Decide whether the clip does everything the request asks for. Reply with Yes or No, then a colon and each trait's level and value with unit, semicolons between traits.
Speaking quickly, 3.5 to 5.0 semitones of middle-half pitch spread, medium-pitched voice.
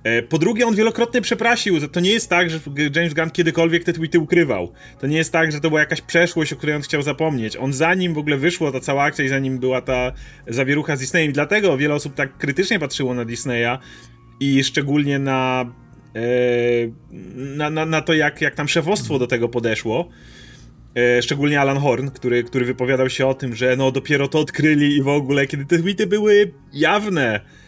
Yes: fast, 195 wpm; average, 4.1 semitones; medium, 145 Hz